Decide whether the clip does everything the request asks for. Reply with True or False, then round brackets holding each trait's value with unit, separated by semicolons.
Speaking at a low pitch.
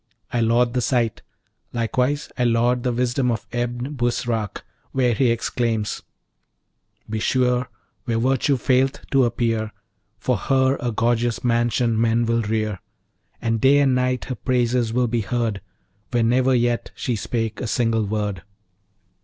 True (120 Hz)